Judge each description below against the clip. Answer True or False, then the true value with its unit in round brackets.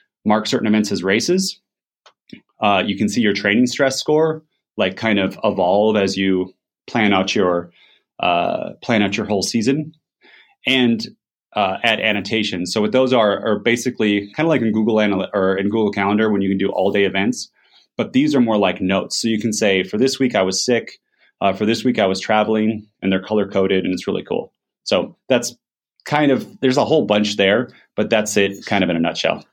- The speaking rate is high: True (210 wpm)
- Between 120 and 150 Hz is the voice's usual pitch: False (105 Hz)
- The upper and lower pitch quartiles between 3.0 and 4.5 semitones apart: True (4.2 semitones)